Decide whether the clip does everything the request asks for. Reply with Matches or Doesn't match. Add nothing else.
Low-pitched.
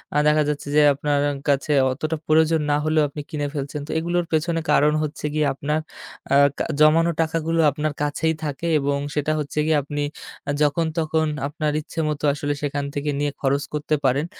Doesn't match